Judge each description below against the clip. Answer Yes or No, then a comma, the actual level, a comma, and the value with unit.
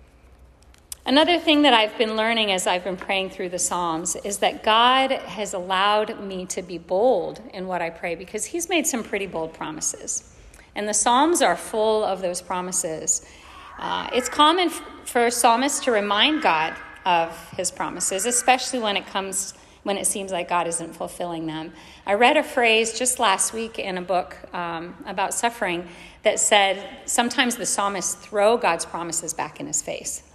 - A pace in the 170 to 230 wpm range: Yes, average, 180 wpm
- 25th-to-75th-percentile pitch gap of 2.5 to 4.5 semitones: No, average, 5.1 semitones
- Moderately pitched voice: No, high, 200 Hz